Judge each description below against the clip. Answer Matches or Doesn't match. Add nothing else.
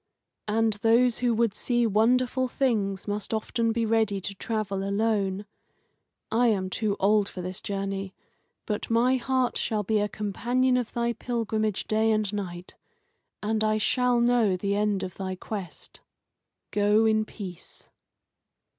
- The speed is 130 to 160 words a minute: Matches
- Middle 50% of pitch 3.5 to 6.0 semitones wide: Doesn't match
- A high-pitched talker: Matches